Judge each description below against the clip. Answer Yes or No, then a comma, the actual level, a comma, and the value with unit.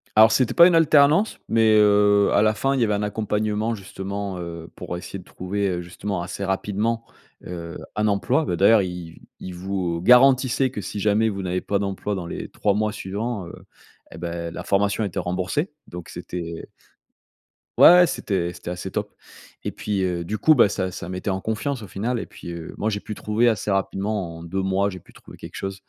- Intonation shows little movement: No, average, 3.2 semitones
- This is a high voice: No, low, 100 Hz